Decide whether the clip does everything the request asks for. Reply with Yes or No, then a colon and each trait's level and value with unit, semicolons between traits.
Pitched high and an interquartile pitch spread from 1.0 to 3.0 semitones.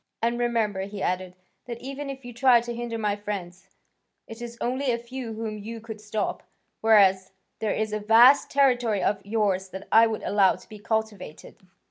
Yes: high, 220 Hz; average, 2.7 semitones